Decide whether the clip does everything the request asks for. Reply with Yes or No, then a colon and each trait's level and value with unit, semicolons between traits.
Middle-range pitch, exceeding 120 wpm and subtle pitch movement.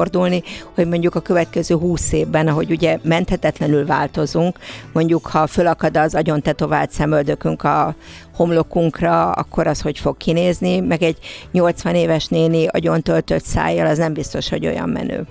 Yes: medium, 165 Hz; average, 150 wpm; narrow, 1.8 semitones